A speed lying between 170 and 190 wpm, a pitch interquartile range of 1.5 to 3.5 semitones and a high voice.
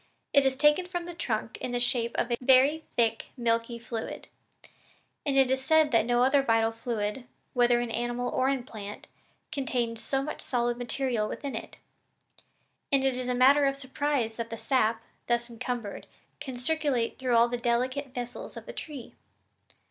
Yes: average, 180 wpm; narrow, 2.4 semitones; high, 245 Hz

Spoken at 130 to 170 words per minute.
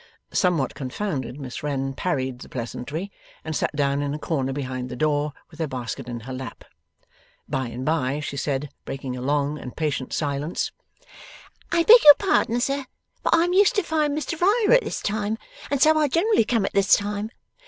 No: average, 195 wpm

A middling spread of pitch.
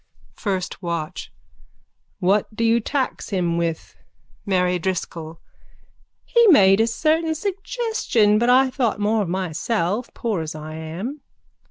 No: wide, 6.2 semitones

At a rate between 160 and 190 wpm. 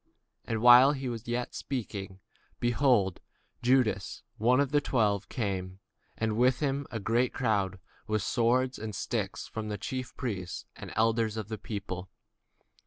No: average, 145 wpm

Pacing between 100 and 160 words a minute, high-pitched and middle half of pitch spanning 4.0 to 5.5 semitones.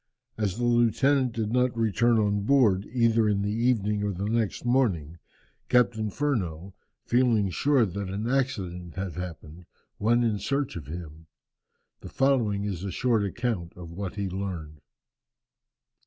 No: average, 150 wpm; low, 105 Hz; average, 4.4 semitones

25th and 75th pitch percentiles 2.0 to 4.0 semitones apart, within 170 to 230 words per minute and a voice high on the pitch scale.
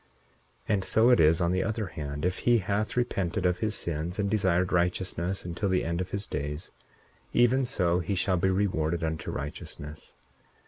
No: average, 3.3 semitones; average, 185 wpm; very low, 90 Hz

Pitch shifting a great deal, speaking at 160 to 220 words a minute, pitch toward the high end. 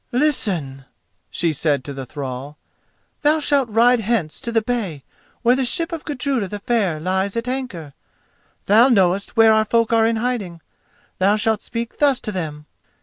Yes: wide, 6.3 semitones; average, 170 wpm; high, 220 Hz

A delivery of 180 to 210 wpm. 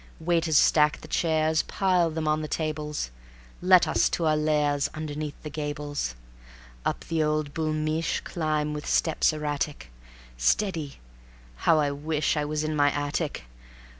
No: average, 150 wpm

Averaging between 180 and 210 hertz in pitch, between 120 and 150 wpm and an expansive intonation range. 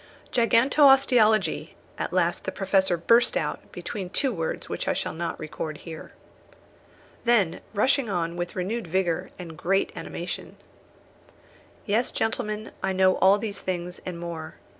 No: high, 190 Hz; average, 140 wpm; average, 4.5 semitones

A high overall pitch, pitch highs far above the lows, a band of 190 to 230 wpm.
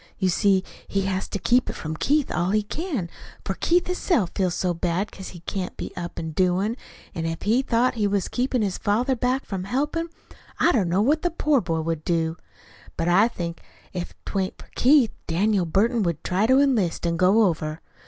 Yes: high, 195 Hz; wide, 6.0 semitones; fast, 205 wpm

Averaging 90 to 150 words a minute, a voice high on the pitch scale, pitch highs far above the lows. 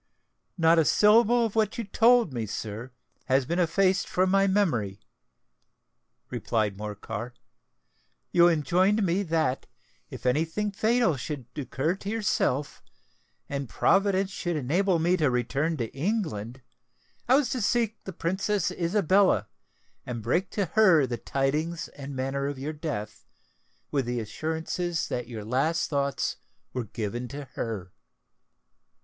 No: average, 140 wpm; medium, 160 Hz; wide, 7.3 semitones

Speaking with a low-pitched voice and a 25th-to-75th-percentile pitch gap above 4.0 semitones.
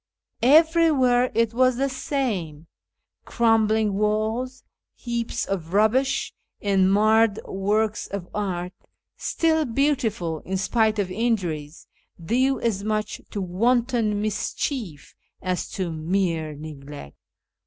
No: high, 215 Hz; average, 4.7 semitones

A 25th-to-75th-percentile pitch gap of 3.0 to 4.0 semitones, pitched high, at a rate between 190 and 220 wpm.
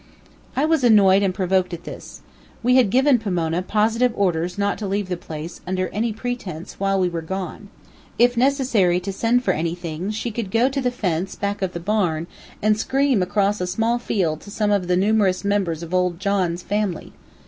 Yes: average, 3.7 semitones; high, 195 Hz; average, 195 wpm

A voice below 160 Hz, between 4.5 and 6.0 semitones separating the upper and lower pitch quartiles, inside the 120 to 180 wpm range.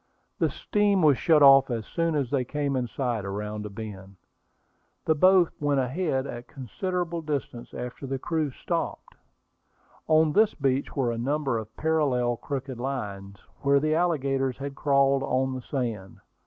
No: low, 135 Hz; average, 3.9 semitones; average, 160 wpm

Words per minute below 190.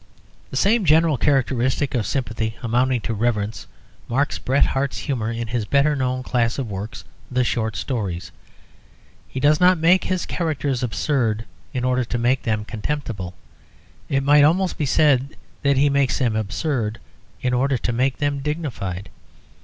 Yes: average, 160 wpm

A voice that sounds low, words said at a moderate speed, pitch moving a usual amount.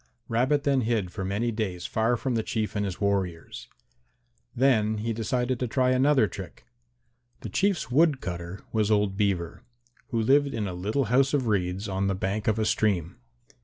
Yes: low, 110 Hz; average, 180 wpm; average, 4.5 semitones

